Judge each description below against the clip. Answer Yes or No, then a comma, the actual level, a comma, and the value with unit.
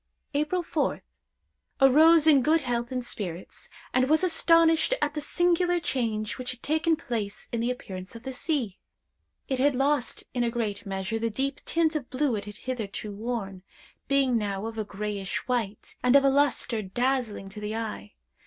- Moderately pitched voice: No, very high, 250 Hz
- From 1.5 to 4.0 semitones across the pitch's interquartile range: No, wide, 5.4 semitones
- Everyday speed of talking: Yes, average, 180 wpm